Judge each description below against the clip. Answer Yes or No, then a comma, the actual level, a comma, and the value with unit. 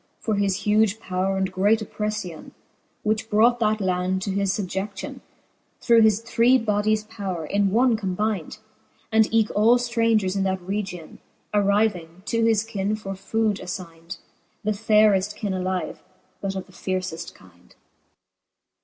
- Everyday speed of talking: Yes, average, 145 wpm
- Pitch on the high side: Yes, high, 205 Hz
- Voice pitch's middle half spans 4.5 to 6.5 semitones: No, narrow, 2.6 semitones